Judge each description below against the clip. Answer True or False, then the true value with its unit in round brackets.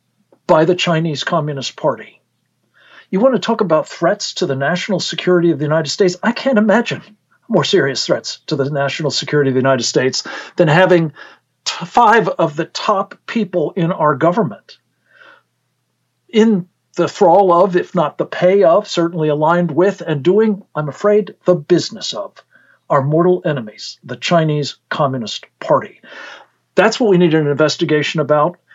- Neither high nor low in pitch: True (170 Hz)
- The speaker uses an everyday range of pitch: True (4.1 semitones)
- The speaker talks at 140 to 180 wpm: True (160 wpm)